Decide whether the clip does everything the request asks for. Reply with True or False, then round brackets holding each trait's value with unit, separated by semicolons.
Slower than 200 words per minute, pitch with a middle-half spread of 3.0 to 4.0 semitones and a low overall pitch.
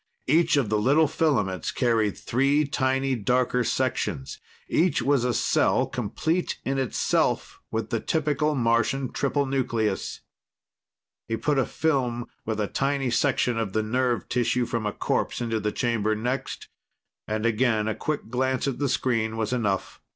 True (155 wpm; 3.6 semitones; 125 Hz)